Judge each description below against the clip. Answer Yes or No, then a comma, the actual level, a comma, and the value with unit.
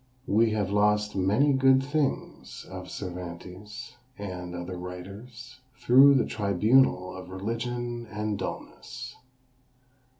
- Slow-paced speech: Yes, slow, 105 wpm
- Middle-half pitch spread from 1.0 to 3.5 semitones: No, average, 4.8 semitones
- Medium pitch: No, low, 105 Hz